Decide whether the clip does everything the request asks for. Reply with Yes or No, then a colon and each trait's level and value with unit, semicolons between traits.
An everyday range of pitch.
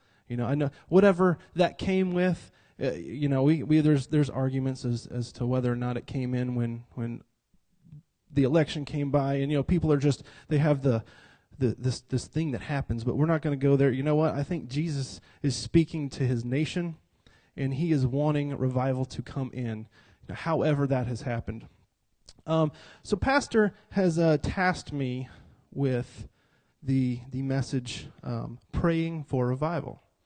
Yes: average, 3.8 semitones